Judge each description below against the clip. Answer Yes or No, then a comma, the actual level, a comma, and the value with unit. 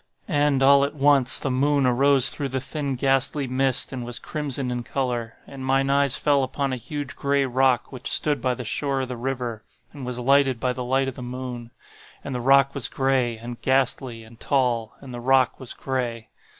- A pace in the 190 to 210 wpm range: Yes, average, 200 wpm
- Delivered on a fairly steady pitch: Yes, narrow, 1.9 semitones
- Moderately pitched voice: No, low, 130 Hz